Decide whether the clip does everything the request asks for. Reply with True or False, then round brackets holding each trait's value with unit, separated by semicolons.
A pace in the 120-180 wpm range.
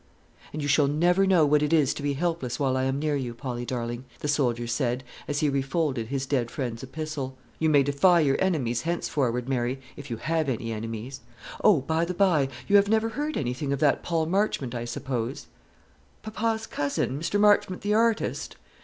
False (200 wpm)